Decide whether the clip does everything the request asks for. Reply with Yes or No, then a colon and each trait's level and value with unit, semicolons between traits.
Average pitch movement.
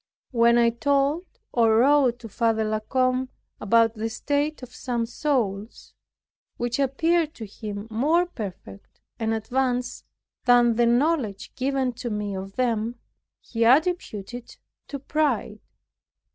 Yes: average, 3.6 semitones